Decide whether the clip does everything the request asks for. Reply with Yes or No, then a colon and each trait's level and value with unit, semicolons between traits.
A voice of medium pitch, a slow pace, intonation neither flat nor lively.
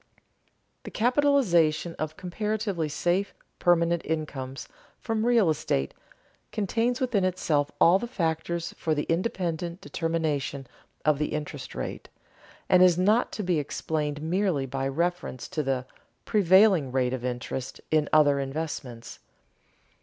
Yes: medium, 165 Hz; slow, 125 wpm; average, 4.4 semitones